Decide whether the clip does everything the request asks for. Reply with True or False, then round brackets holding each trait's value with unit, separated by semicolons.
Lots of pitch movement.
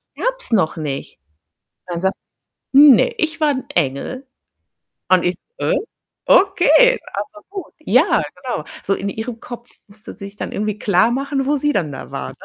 True (7.5 semitones)